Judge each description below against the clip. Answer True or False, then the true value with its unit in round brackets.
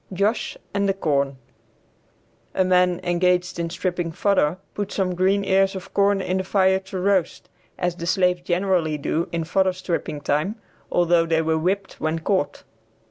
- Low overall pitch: False (180 Hz)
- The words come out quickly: False (165 wpm)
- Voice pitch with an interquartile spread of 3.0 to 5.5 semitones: False (2.4 semitones)